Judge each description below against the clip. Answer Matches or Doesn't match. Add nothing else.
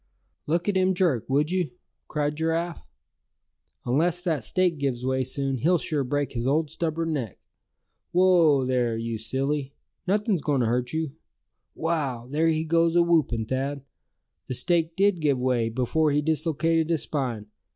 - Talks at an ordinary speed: Matches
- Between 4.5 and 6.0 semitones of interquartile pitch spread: Doesn't match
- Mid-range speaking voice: Matches